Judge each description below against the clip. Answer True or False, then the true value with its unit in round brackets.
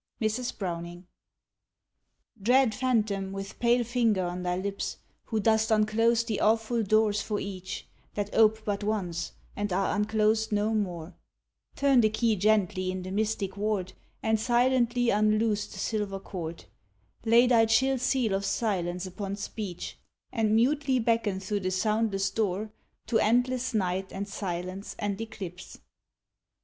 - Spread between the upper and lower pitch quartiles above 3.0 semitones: False (2.7 semitones)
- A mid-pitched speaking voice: False (215 Hz)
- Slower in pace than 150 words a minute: True (140 wpm)